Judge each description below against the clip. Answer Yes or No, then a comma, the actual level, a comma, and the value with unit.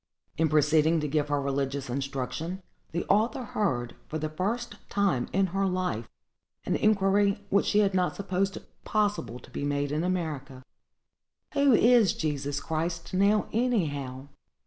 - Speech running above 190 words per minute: No, average, 145 wpm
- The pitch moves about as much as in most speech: No, wide, 5.8 semitones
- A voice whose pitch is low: No, medium, 170 Hz